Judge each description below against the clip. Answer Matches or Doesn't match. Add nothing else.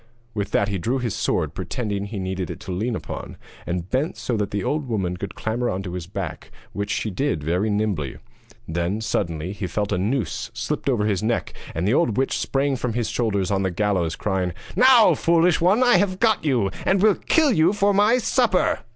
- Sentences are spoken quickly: Matches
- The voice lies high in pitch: Doesn't match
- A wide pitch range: Matches